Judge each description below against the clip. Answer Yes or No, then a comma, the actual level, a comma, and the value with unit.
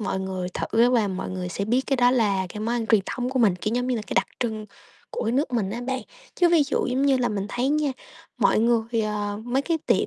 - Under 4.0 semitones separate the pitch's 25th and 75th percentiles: Yes, average, 3.5 semitones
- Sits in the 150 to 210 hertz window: No, high, 230 Hz